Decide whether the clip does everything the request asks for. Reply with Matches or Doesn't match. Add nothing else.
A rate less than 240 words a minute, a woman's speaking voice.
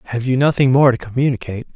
Doesn't match